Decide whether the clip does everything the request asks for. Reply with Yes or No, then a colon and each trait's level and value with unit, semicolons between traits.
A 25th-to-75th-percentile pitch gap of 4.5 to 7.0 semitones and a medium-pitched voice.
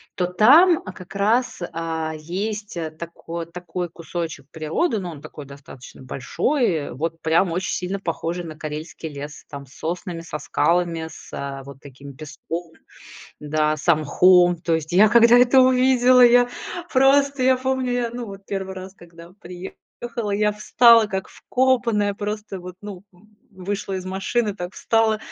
Yes: average, 5.2 semitones; medium, 180 Hz